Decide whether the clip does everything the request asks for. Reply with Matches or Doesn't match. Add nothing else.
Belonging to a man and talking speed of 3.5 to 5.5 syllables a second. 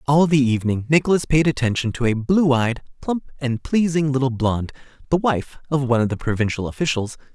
Doesn't match